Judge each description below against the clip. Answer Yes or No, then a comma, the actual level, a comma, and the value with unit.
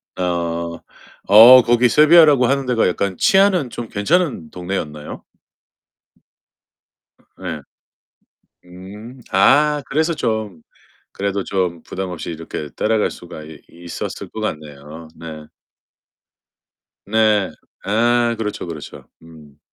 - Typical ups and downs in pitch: No, wide, 6.4 semitones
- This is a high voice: No, low, 100 Hz